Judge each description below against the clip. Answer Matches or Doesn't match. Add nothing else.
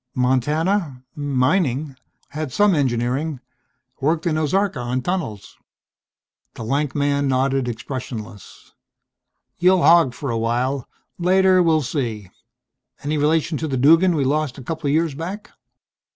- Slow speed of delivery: Matches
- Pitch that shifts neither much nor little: Matches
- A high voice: Doesn't match